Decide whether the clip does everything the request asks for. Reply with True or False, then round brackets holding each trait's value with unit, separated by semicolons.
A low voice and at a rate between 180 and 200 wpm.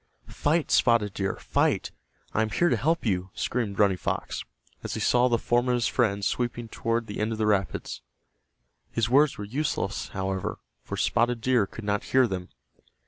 True (115 Hz; 185 wpm)